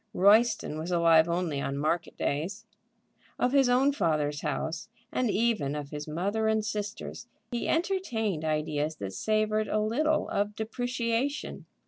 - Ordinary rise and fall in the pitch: No, wide, 6.7 semitones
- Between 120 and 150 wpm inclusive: Yes, average, 140 wpm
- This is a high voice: Yes, high, 205 Hz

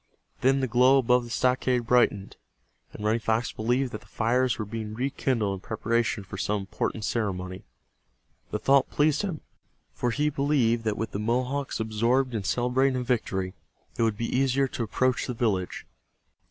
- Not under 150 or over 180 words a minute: Yes, average, 170 wpm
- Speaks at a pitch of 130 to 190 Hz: No, low, 120 Hz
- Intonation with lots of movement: No, average, 3.0 semitones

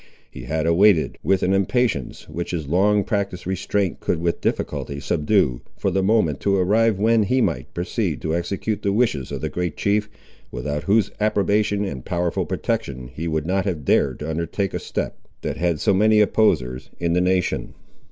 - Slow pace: No, average, 180 wpm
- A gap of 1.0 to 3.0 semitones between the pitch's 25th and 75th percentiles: No, average, 4.4 semitones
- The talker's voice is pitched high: No, very low, 90 Hz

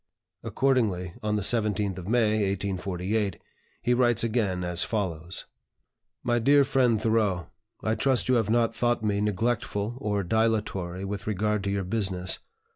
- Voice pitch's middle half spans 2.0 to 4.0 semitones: Yes, average, 3.1 semitones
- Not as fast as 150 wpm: Yes, average, 140 wpm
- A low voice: Yes, low, 105 Hz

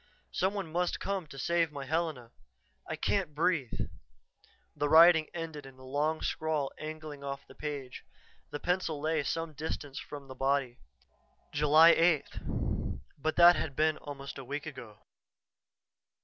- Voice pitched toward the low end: No, medium, 150 Hz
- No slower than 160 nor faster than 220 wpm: No, average, 150 wpm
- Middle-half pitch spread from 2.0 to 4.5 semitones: Yes, average, 2.9 semitones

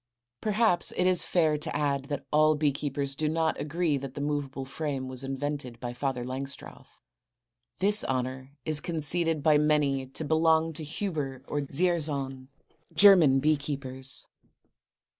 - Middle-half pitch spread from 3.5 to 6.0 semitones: No, average, 2.9 semitones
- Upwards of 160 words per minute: No, average, 145 wpm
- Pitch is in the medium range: Yes, medium, 145 Hz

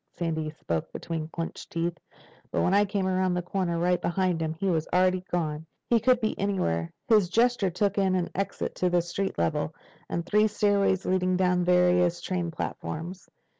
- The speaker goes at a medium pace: Yes, average, 170 wpm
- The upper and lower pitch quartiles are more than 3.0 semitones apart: No, narrow, 2.5 semitones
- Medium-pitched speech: Yes, medium, 180 Hz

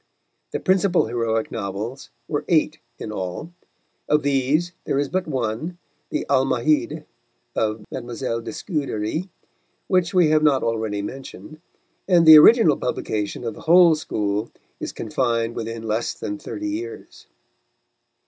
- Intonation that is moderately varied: No, wide, 6.4 semitones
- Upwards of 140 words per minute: No, slow, 135 wpm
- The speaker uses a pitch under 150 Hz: Yes, low, 135 Hz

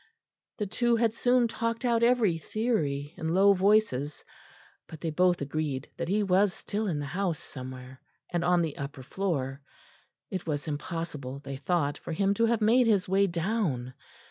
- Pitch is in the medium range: Yes, medium, 175 Hz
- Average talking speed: Yes, average, 170 wpm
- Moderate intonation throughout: No, wide, 6.6 semitones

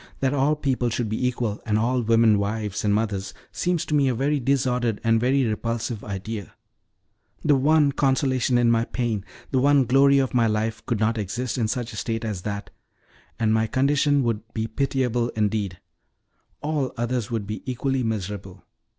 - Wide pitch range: No, average, 3.5 semitones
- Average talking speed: Yes, average, 180 wpm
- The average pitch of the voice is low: Yes, low, 120 Hz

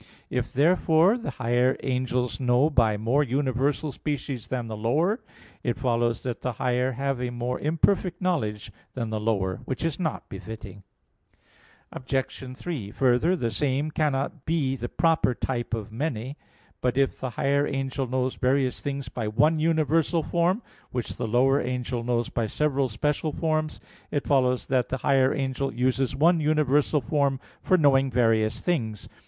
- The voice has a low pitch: Yes, low, 130 Hz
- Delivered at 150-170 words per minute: Yes, average, 160 wpm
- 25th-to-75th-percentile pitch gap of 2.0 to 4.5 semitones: Yes, average, 3.6 semitones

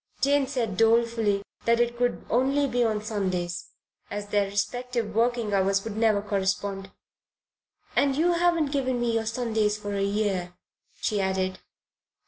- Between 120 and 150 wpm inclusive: Yes, average, 145 wpm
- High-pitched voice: Yes, high, 220 Hz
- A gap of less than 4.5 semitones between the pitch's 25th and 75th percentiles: Yes, average, 3.4 semitones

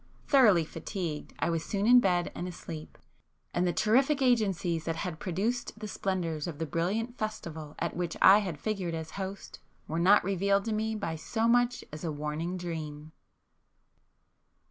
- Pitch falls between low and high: Yes, medium, 180 Hz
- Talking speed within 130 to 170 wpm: Yes, average, 165 wpm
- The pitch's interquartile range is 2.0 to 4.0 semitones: No, average, 4.7 semitones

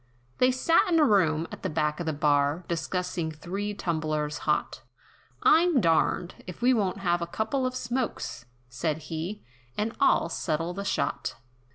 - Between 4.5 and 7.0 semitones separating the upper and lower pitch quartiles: Yes, wide, 5.6 semitones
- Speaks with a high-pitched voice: No, medium, 175 Hz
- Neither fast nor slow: Yes, average, 165 wpm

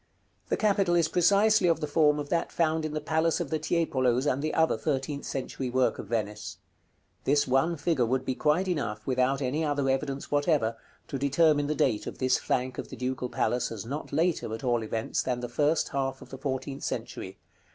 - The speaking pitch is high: No, medium, 140 Hz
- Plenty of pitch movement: No, average, 3.6 semitones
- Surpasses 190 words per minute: Yes, fast, 205 wpm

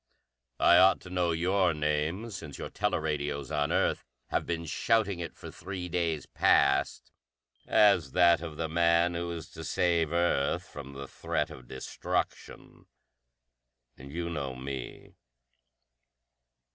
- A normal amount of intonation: Yes, average, 3.1 semitones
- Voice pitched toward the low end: Yes, very low, 85 Hz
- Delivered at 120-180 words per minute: Yes, slow, 135 wpm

